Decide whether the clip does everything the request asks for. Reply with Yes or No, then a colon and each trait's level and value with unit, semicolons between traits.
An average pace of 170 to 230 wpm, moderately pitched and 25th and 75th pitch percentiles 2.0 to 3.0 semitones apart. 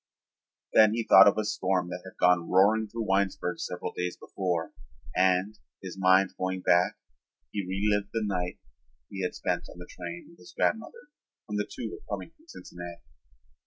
No: average, 175 wpm; very low, 95 Hz; average, 2.7 semitones